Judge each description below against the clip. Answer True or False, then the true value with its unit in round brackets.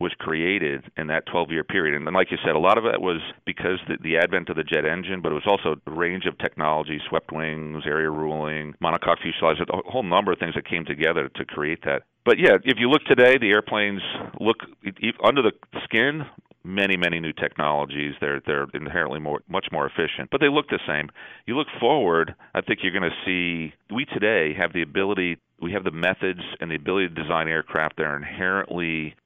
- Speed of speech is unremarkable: False (215 wpm)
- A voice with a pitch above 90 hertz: False (80 Hz)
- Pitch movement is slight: False (3.5 semitones)